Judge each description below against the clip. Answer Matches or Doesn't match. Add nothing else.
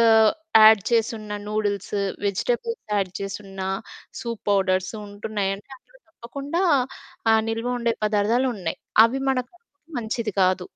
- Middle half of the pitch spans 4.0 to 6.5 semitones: Doesn't match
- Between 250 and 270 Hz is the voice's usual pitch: Doesn't match